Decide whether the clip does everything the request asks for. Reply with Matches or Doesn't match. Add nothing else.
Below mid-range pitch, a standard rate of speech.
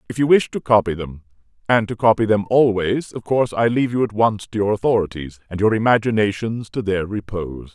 Doesn't match